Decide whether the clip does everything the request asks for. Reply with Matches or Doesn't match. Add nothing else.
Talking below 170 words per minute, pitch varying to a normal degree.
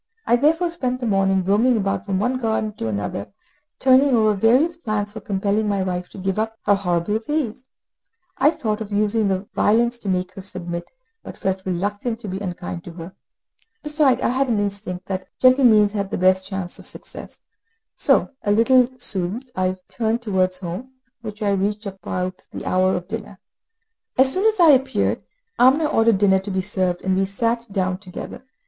Doesn't match